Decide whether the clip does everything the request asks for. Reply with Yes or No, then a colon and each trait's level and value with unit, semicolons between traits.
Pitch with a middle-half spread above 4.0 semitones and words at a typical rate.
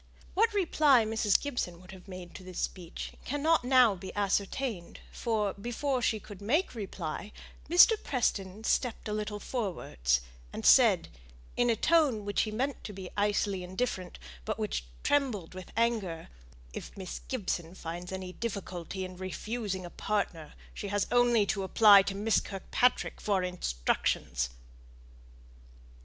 Yes: average, 4.5 semitones; average, 145 wpm